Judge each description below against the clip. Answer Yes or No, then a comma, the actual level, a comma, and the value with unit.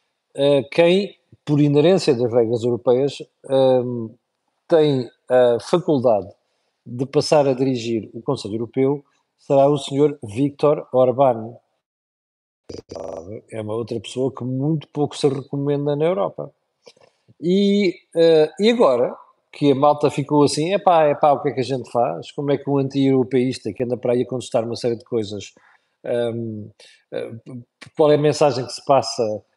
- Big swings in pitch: No, average, 3.5 semitones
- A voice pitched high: No, low, 135 Hz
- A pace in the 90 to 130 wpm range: No, average, 145 wpm